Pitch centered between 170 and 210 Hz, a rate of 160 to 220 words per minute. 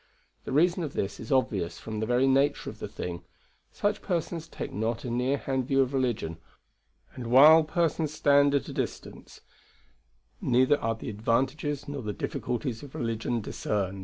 No: low, 130 Hz; average, 170 wpm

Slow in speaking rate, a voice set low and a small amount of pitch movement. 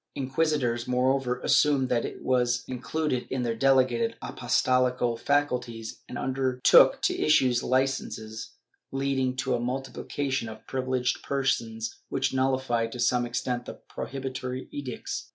Yes: slow, 125 wpm; low, 130 Hz; narrow, 1.6 semitones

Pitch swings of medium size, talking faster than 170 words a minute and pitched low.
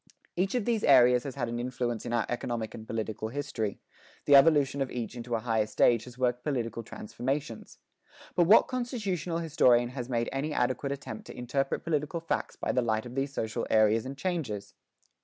Yes: average, 3.9 semitones; average, 190 wpm; low, 125 Hz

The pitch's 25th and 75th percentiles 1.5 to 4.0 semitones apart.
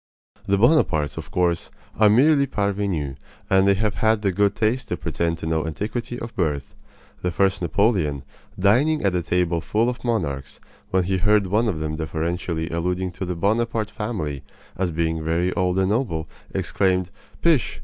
No: average, 4.5 semitones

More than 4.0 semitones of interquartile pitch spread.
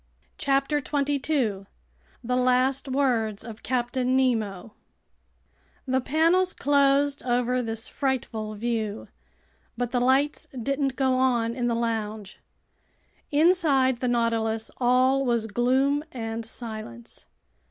No: average, 3.2 semitones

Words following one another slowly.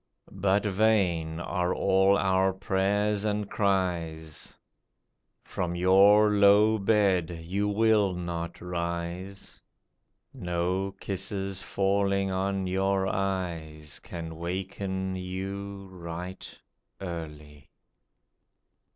Yes: slow, 85 wpm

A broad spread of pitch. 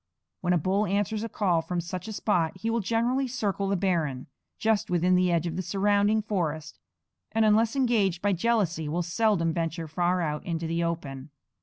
No: average, 4.2 semitones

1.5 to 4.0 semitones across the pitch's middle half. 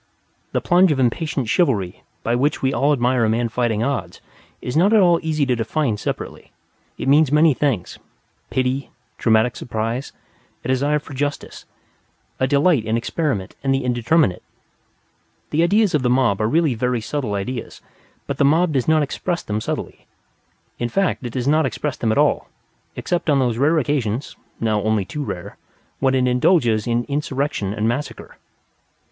No: average, 4.5 semitones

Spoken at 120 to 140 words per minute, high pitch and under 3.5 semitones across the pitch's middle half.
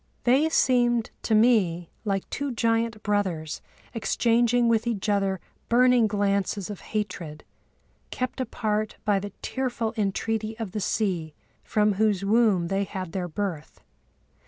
Yes: slow, 135 wpm; high, 210 Hz; average, 3.1 semitones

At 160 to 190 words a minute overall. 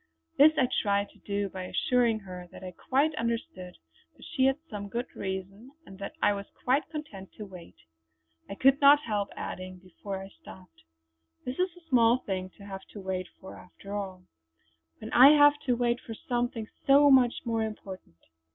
Yes: average, 185 wpm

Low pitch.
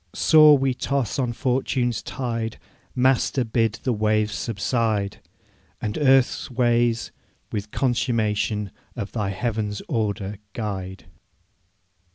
Yes: low, 115 Hz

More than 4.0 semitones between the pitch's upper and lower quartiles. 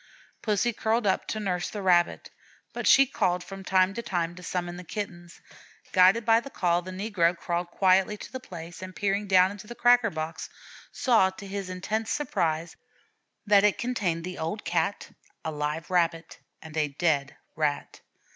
No: average, 3.4 semitones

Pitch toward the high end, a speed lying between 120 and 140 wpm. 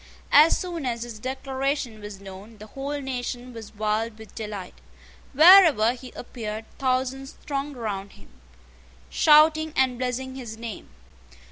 Yes: very high, 250 Hz; slow, 135 wpm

